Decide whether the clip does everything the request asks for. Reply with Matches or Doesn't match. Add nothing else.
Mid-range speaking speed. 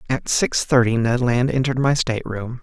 Matches